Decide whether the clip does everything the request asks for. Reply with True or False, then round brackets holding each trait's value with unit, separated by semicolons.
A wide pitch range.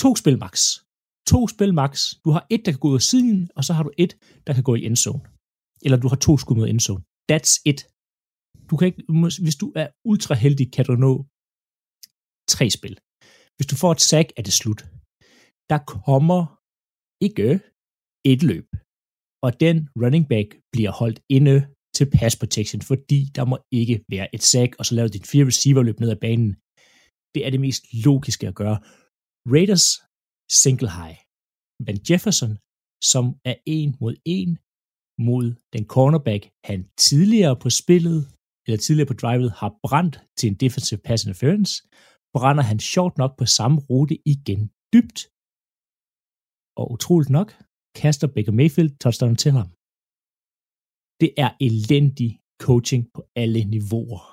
True (5.7 semitones)